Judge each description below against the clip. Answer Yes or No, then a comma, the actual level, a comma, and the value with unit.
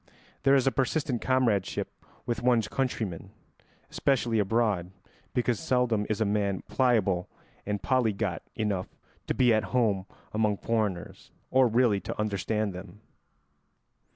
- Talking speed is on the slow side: Yes, slow, 125 wpm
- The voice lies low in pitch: Yes, low, 110 Hz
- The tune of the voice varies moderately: Yes, average, 3.6 semitones